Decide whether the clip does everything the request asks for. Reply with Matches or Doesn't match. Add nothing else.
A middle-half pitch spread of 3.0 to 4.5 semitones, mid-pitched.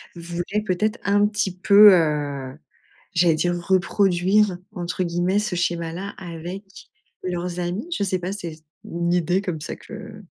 Doesn't match